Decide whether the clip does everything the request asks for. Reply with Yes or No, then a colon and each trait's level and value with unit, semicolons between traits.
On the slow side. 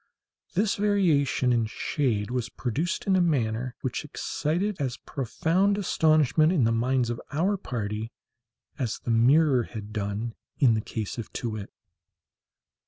No: average, 145 wpm